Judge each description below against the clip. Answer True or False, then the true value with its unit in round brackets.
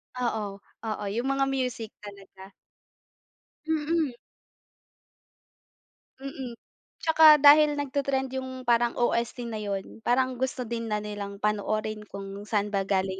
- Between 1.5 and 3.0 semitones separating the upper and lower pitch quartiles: False (4.2 semitones)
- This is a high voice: True (235 Hz)